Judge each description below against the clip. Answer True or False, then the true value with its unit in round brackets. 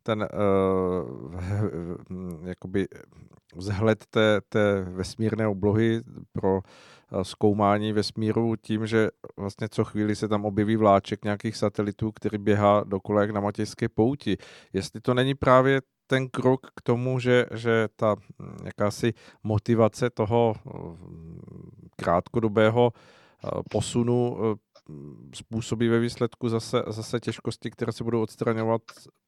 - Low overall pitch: True (110 Hz)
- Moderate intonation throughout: False (2.3 semitones)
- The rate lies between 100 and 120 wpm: True (115 wpm)